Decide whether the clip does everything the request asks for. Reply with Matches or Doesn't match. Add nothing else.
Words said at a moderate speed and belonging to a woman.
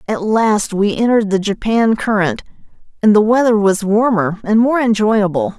Matches